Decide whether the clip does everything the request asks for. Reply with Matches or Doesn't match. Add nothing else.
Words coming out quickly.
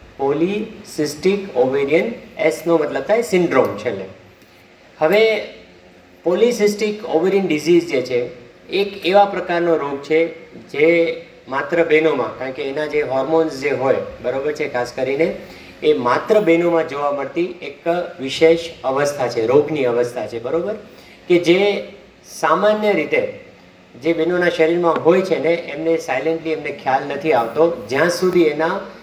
Doesn't match